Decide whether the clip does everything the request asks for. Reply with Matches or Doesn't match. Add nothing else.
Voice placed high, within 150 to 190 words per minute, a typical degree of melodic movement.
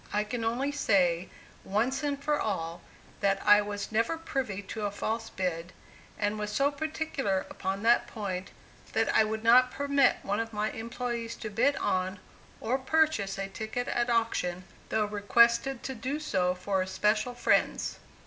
Matches